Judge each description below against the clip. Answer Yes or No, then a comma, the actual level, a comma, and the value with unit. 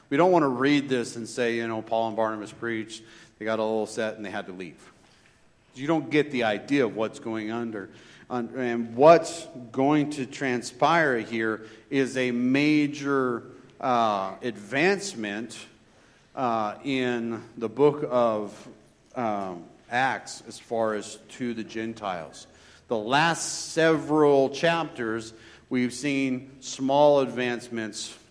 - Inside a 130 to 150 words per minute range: Yes, average, 140 wpm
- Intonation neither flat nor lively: Yes, average, 4.0 semitones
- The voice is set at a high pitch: No, low, 120 Hz